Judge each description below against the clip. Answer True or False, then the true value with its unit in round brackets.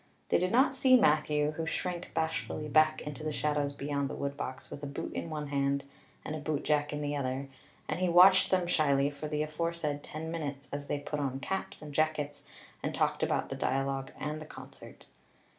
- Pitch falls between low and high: True (150 Hz)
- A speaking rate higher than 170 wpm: True (200 wpm)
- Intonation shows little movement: True (1.8 semitones)